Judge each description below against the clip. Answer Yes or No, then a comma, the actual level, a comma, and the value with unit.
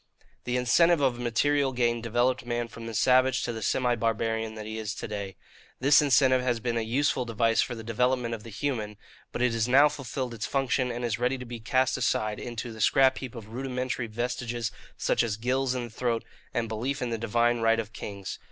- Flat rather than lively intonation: Yes, narrow, 2.1 semitones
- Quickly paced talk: Yes, fast, 215 wpm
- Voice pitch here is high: No, low, 120 Hz